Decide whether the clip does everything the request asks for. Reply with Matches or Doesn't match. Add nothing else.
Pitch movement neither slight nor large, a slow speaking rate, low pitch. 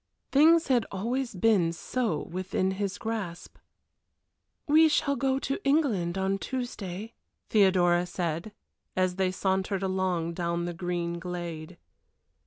Doesn't match